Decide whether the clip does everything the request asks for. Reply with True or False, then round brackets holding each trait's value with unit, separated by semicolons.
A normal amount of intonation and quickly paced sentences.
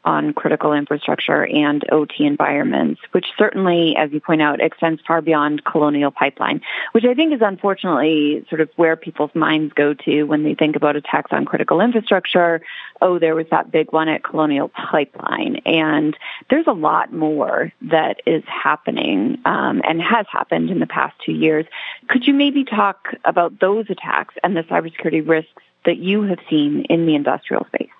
False (4.3 semitones; 175 wpm)